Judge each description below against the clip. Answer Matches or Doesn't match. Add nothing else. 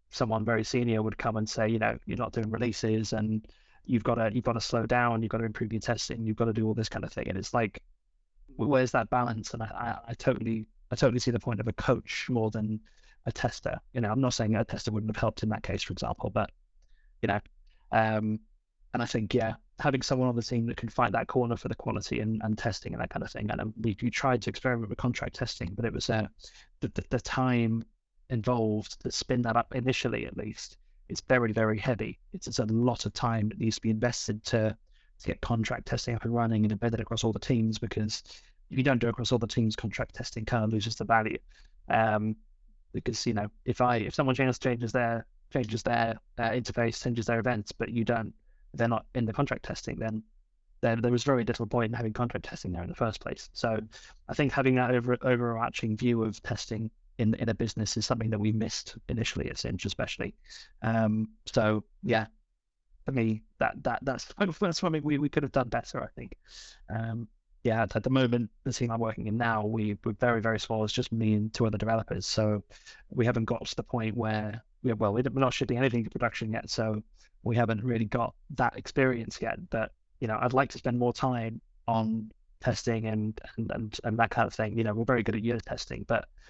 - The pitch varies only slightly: Matches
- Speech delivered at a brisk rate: Matches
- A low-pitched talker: Matches